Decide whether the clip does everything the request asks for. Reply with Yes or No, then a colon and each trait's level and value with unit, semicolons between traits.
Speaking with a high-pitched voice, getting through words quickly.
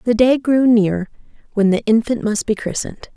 No: high, 220 Hz; average, 190 wpm